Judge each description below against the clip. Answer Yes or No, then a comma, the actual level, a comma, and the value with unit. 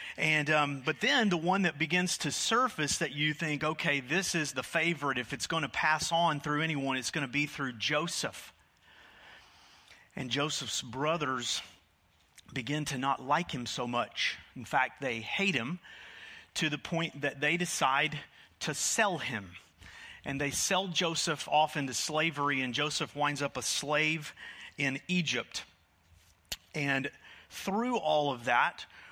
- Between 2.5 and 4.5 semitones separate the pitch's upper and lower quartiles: Yes, average, 3.6 semitones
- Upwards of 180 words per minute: No, average, 155 wpm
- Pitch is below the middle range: No, medium, 145 Hz